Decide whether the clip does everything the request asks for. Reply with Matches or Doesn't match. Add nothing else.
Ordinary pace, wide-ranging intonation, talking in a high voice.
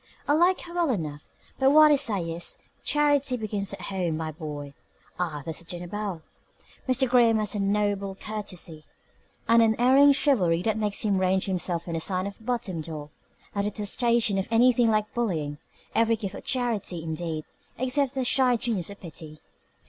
Matches